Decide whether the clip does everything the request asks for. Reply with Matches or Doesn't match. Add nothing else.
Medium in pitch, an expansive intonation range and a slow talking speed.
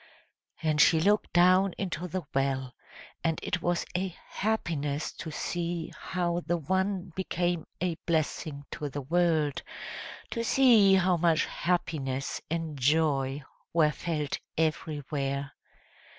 Doesn't match